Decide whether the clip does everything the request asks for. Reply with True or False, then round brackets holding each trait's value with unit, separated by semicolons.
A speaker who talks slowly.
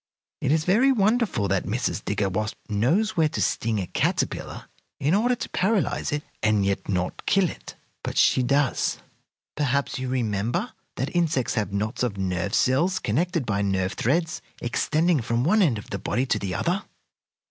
False (175 wpm)